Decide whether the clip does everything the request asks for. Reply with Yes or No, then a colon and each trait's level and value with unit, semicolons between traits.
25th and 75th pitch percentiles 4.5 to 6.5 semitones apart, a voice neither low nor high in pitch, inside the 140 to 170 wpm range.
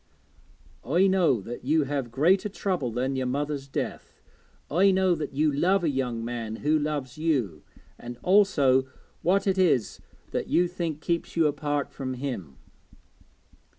Yes: average, 5.1 semitones; medium, 145 Hz; average, 150 wpm